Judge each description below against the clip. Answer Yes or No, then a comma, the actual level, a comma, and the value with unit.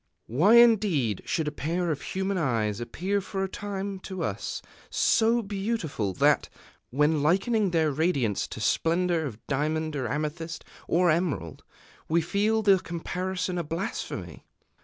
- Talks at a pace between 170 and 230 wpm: No, average, 140 wpm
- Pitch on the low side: No, medium, 170 Hz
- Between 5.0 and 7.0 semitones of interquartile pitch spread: No, average, 4.6 semitones